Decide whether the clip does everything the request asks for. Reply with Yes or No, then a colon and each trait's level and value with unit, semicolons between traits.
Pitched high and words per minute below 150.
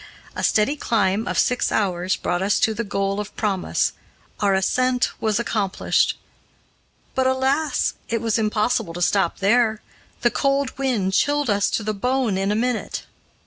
No: high, 220 Hz; average, 160 wpm